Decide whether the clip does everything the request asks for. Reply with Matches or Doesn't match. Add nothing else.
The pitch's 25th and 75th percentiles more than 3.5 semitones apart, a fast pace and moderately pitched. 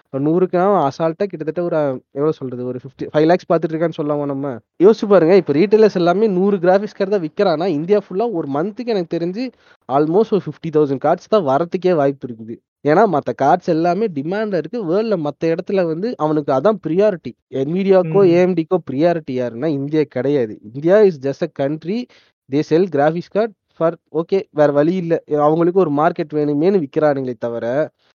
Matches